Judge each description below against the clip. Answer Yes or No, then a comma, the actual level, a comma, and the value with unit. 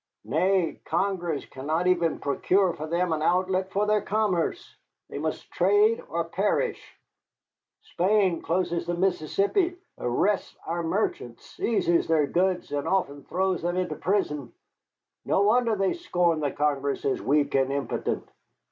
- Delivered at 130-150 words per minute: Yes, average, 140 wpm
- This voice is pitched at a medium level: Yes, medium, 180 Hz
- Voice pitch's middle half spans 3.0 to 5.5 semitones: Yes, average, 4.0 semitones